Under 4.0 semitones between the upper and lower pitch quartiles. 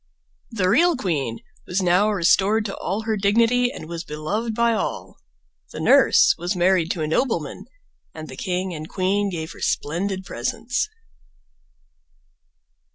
No: average, 4.6 semitones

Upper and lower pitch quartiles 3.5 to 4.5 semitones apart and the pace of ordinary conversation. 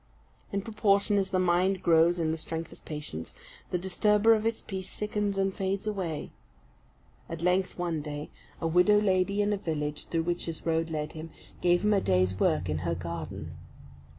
Yes: average, 4.0 semitones; average, 185 wpm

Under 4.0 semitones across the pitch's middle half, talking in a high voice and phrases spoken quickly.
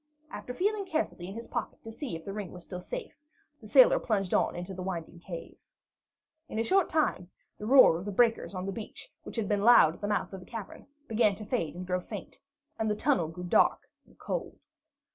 No: average, 5.0 semitones; high, 205 Hz; fast, 225 wpm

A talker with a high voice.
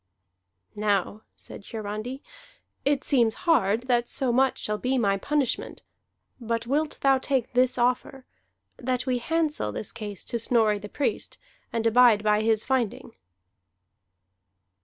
Yes: high, 240 Hz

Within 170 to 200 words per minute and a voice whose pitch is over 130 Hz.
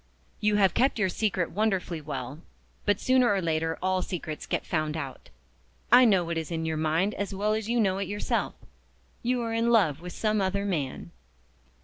Yes: average, 195 wpm; high, 190 Hz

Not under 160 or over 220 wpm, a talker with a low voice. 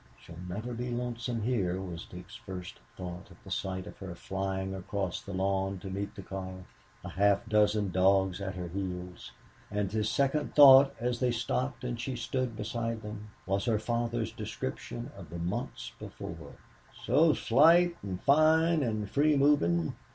Yes: average, 165 wpm; low, 105 Hz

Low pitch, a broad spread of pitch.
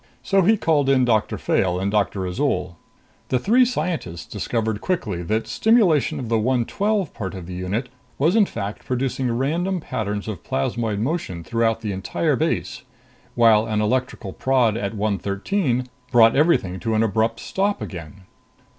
Yes: low, 115 Hz; wide, 5.7 semitones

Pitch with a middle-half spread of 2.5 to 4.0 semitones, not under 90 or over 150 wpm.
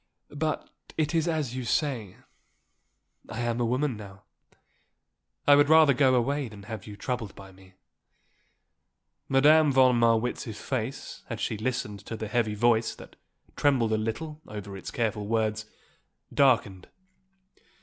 No: average, 4.4 semitones; average, 140 wpm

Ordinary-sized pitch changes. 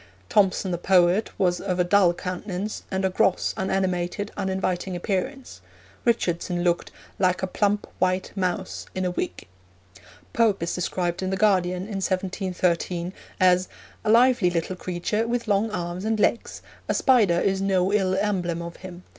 No: narrow, 2.2 semitones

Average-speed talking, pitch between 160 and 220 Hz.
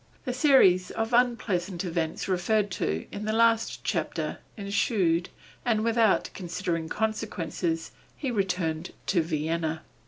No: slow, 120 wpm; high, 190 Hz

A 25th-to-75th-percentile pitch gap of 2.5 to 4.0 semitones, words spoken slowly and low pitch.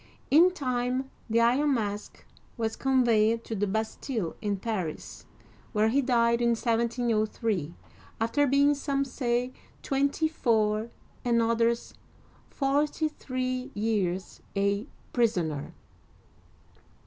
No: average, 3.4 semitones; slow, 105 wpm; high, 235 Hz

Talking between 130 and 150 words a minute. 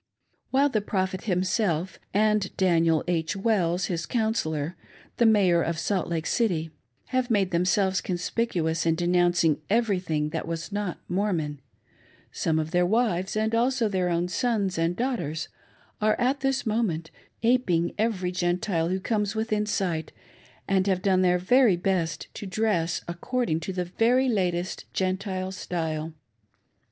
Yes: average, 145 wpm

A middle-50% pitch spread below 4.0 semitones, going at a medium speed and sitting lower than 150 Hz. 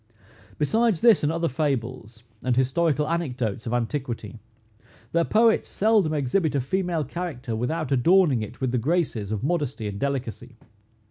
No: wide, 5.6 semitones; average, 145 wpm; medium, 140 Hz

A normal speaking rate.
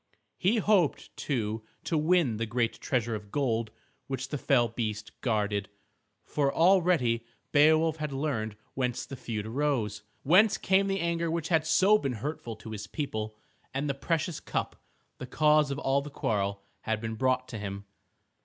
Yes: average, 165 wpm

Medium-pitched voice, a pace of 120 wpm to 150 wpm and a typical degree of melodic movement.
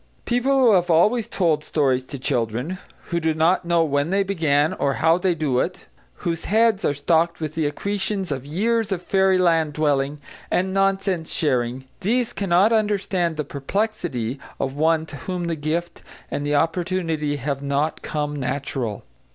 No: medium, 165 Hz; average, 165 wpm; average, 4.7 semitones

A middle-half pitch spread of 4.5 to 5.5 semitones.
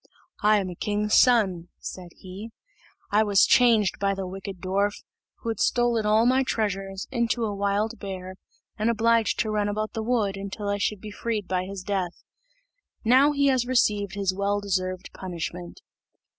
No: narrow, 2.6 semitones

